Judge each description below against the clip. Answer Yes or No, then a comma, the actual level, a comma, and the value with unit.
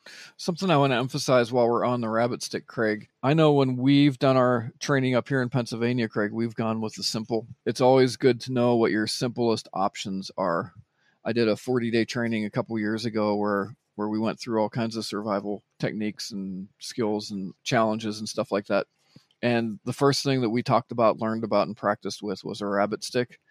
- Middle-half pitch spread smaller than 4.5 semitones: Yes, average, 3.0 semitones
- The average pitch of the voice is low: Yes, low, 115 Hz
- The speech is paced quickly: Yes, fast, 215 wpm